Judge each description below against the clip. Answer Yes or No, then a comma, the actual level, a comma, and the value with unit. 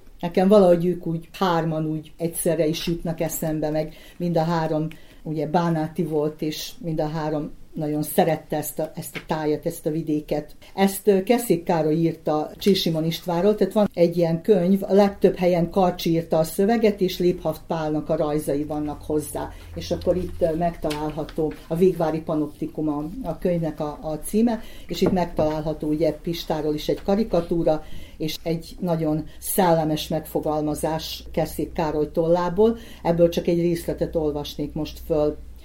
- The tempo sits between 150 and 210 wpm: Yes, fast, 155 wpm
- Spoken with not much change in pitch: Yes, narrow, 2.3 semitones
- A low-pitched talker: No, medium, 165 Hz